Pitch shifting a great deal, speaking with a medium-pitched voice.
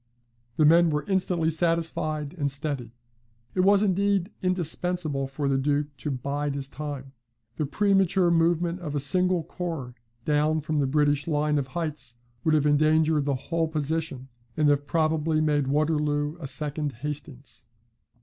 No: narrow, 2.5 semitones; medium, 150 Hz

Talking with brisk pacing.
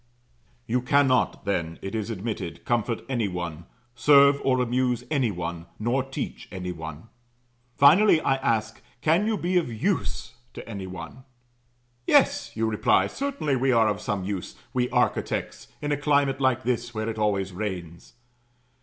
No: average, 155 wpm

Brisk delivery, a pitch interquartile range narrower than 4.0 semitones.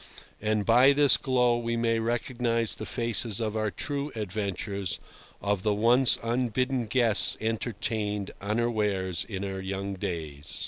No: slow, 135 wpm; average, 2.9 semitones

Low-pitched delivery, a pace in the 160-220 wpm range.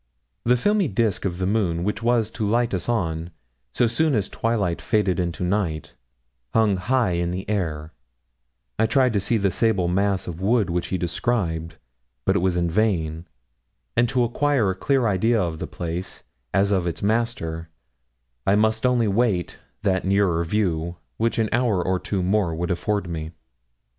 Yes: low, 100 Hz; average, 170 wpm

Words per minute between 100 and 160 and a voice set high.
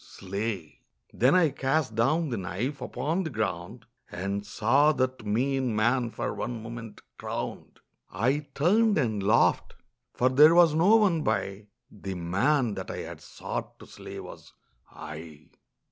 No: average, 145 wpm; low, 120 Hz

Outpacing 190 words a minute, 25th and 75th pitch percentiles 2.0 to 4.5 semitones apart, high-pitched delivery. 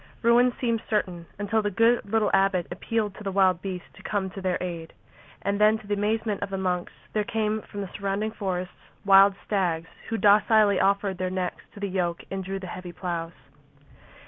Yes: average, 200 wpm; narrow, 2.4 semitones; high, 195 Hz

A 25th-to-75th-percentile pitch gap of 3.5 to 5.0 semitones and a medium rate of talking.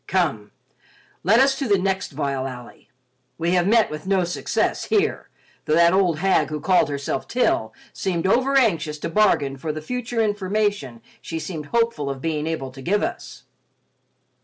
No: wide, 5.5 semitones; average, 165 wpm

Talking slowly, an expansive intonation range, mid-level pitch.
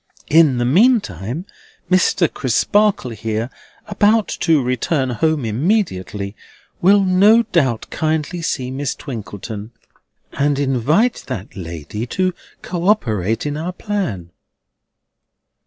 Yes: slow, 105 wpm; wide, 8.4 semitones; medium, 145 Hz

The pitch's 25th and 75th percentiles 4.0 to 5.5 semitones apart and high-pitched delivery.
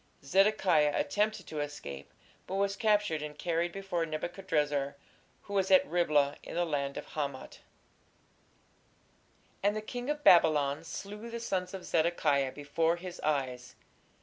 No: average, 5.0 semitones; medium, 170 Hz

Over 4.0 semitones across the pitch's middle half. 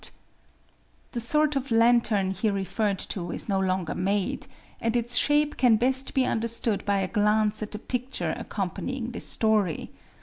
No: average, 3.7 semitones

